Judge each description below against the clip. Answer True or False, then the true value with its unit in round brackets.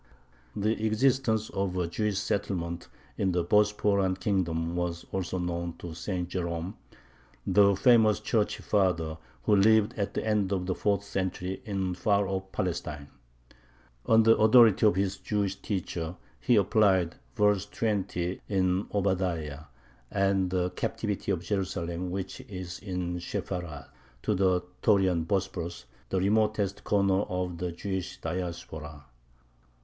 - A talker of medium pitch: False (95 Hz)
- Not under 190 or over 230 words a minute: False (135 wpm)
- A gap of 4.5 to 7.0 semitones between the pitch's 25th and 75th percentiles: False (2.7 semitones)